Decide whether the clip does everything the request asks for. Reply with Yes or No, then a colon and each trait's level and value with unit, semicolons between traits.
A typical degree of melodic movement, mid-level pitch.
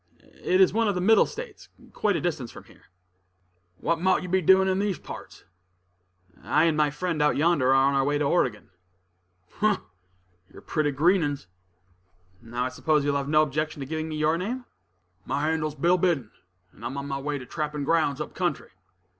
Yes: average, 4.3 semitones; medium, 155 Hz